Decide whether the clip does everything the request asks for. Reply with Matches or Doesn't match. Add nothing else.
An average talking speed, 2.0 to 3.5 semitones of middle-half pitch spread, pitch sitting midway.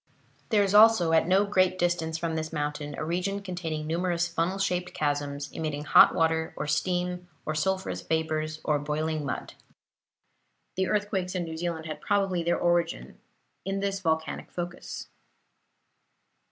Matches